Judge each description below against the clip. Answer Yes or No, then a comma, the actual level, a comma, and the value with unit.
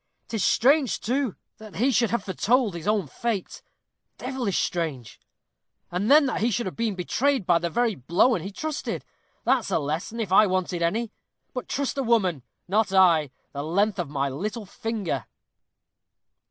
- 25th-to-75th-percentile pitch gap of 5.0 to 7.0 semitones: Yes, average, 5.3 semitones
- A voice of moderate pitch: No, high, 205 Hz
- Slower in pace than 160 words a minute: No, average, 165 wpm